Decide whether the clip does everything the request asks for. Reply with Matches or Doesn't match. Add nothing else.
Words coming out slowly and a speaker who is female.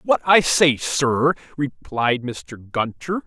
Doesn't match